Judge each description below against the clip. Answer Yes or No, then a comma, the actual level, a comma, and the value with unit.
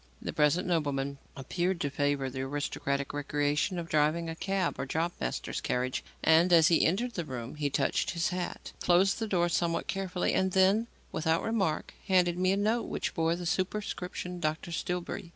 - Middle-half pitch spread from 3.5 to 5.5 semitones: Yes, average, 4.0 semitones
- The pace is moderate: Yes, average, 180 wpm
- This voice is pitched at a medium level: Yes, medium, 170 Hz